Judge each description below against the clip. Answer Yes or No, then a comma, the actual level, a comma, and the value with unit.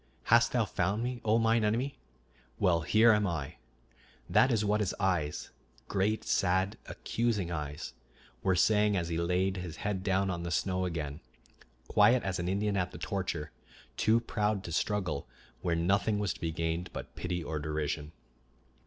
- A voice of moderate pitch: No, very low, 95 Hz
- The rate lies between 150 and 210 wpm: Yes, average, 170 wpm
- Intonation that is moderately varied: Yes, average, 3.7 semitones